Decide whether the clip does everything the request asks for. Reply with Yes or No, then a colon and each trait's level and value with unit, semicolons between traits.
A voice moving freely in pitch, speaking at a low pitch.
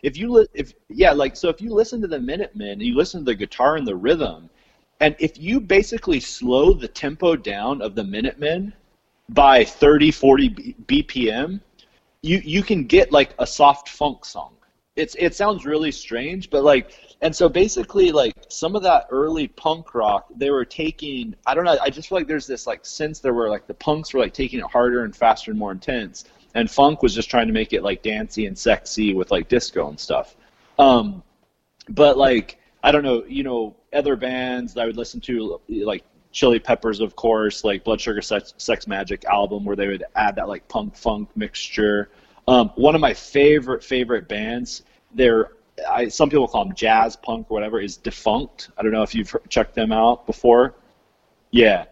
No: wide, 9.0 semitones; medium, 145 Hz